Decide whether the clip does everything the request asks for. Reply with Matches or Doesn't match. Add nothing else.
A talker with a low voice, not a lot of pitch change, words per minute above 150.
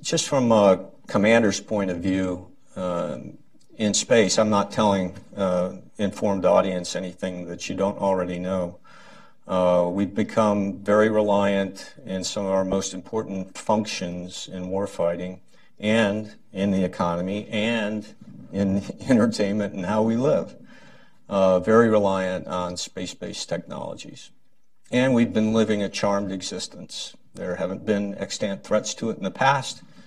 Doesn't match